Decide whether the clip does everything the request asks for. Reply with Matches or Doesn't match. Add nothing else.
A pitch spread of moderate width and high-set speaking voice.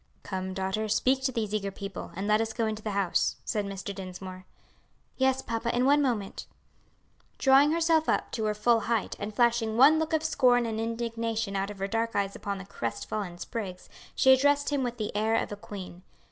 Matches